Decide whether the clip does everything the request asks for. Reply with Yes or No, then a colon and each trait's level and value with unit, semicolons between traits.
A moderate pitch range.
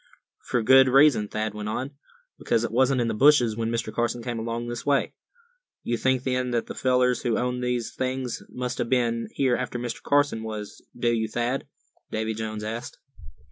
No: narrow, 2.2 semitones